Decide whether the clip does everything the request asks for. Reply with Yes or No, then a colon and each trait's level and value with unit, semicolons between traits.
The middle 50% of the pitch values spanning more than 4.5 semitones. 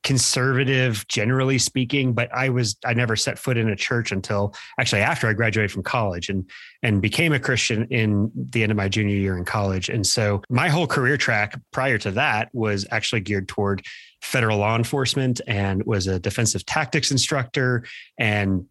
No: average, 3.9 semitones